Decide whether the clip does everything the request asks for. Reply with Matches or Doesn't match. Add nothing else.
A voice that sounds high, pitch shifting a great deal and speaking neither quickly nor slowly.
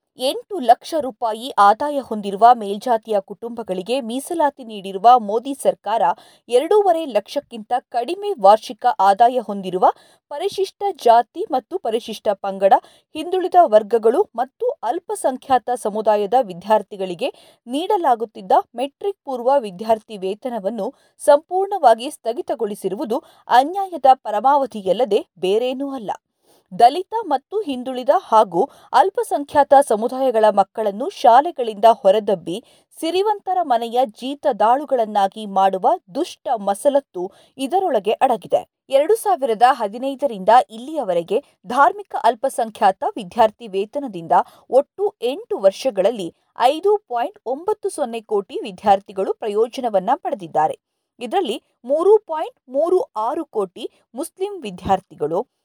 Matches